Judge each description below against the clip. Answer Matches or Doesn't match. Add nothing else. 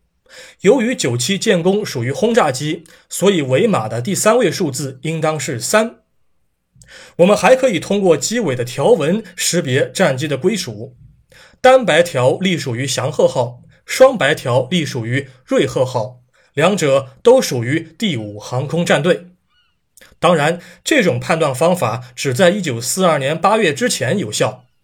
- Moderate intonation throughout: Doesn't match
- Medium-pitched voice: Matches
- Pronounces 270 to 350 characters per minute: Doesn't match